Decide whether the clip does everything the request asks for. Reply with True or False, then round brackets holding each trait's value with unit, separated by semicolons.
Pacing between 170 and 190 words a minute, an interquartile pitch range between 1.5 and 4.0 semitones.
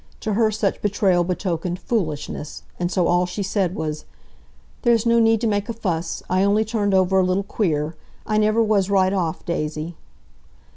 True (180 wpm; 3.4 semitones)